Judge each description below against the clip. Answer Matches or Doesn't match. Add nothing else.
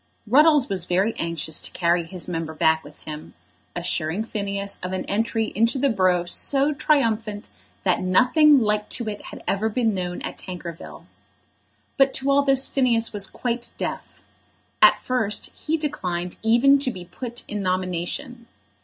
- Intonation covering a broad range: Matches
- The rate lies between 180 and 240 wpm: Doesn't match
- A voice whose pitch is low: Doesn't match